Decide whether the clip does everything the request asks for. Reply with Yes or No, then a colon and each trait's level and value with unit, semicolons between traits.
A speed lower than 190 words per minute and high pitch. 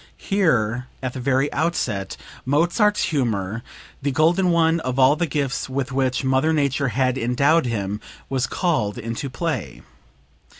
No: average, 140 wpm; low, 135 Hz